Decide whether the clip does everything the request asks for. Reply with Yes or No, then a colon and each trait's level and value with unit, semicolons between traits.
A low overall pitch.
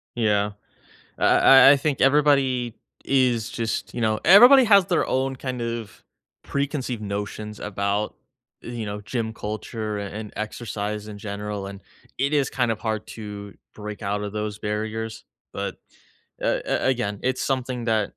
Yes: low, 110 Hz